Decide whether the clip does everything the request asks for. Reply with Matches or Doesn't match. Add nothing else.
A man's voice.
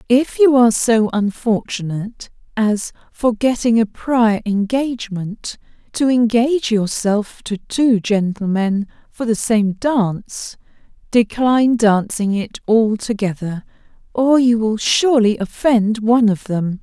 Doesn't match